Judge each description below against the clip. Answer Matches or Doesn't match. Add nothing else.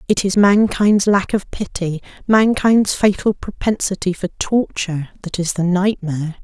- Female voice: Matches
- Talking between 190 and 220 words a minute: Doesn't match